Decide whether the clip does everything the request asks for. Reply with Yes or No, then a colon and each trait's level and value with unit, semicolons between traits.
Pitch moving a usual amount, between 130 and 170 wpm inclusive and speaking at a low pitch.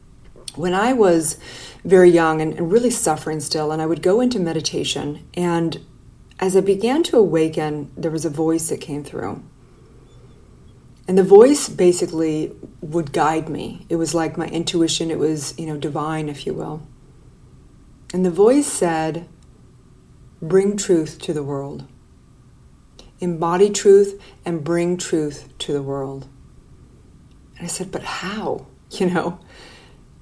No: average, 3.0 semitones; average, 145 wpm; medium, 165 Hz